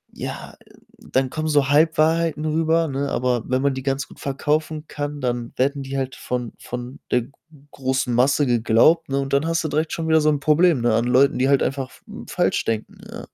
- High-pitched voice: No, medium, 140 Hz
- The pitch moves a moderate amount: Yes, average, 3.3 semitones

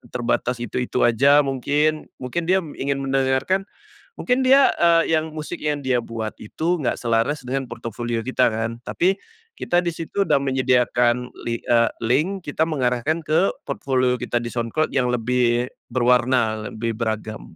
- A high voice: No, low, 130 Hz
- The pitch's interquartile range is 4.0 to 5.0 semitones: Yes, average, 4.6 semitones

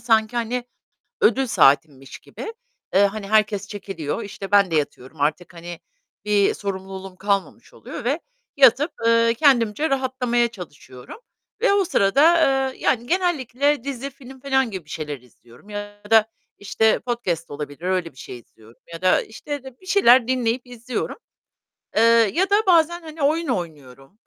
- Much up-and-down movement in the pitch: Yes, wide, 6.4 semitones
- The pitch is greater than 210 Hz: Yes, high, 220 Hz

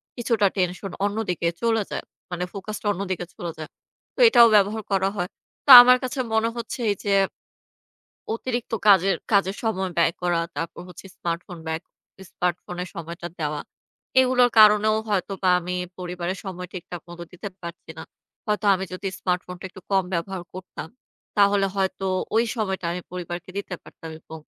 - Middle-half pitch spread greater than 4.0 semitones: No, average, 3.0 semitones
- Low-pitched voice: No, high, 190 Hz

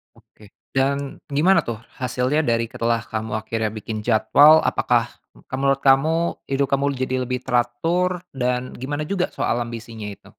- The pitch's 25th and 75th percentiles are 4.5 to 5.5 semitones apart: No, average, 3.3 semitones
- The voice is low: Yes, low, 125 Hz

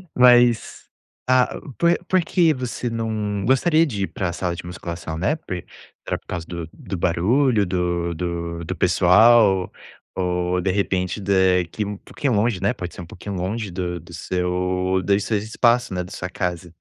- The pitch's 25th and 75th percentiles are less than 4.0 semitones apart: No, average, 4.3 semitones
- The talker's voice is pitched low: Yes, very low, 95 Hz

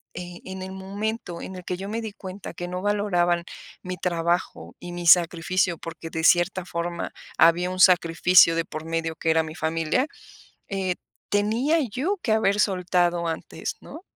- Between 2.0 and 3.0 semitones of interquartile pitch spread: Yes, average, 2.7 semitones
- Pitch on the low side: No, medium, 180 Hz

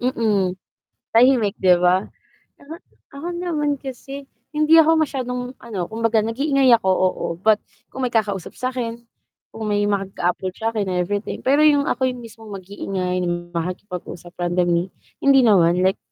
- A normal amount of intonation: No, wide, 5.8 semitones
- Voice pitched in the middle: No, high, 220 Hz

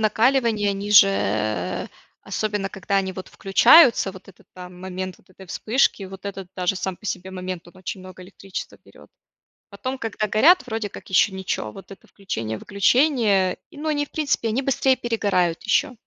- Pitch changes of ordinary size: Yes, average, 3.4 semitones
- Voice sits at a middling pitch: No, high, 195 Hz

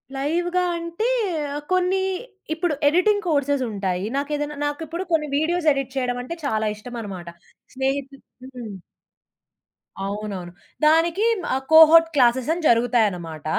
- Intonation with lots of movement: Yes, wide, 5.9 semitones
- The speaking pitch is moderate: No, very high, 280 Hz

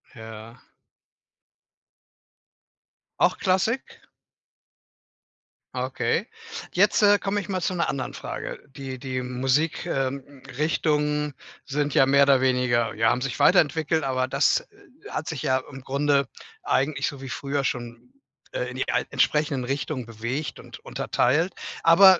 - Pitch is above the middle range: No, medium, 140 Hz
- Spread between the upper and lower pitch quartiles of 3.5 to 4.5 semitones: Yes, average, 4.0 semitones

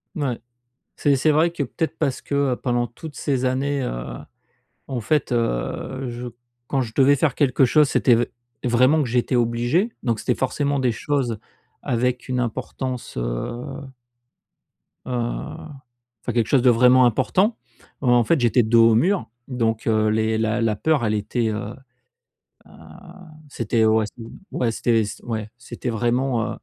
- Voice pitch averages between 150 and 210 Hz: No, low, 120 Hz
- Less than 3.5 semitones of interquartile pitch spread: Yes, average, 2.9 semitones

